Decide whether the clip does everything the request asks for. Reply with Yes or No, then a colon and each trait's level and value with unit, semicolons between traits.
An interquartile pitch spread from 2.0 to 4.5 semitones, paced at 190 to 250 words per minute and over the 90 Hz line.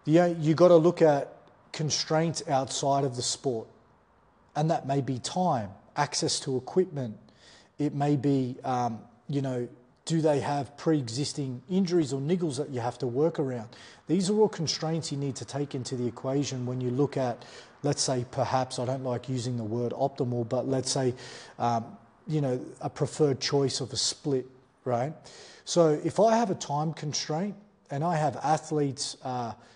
No: average, 3.6 semitones; average, 180 wpm; medium, 140 Hz